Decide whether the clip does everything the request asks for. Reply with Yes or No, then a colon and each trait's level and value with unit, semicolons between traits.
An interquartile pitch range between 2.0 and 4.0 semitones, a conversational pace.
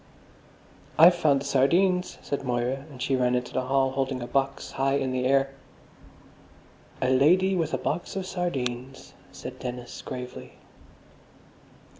Yes: average, 3.3 semitones; average, 145 wpm